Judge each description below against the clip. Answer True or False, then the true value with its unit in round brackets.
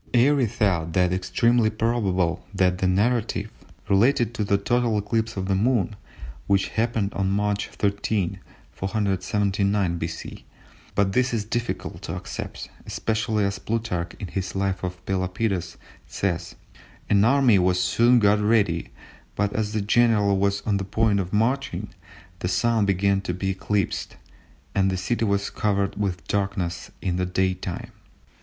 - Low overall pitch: True (100 Hz)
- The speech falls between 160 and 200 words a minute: False (145 wpm)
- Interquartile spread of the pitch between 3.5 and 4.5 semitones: False (2.8 semitones)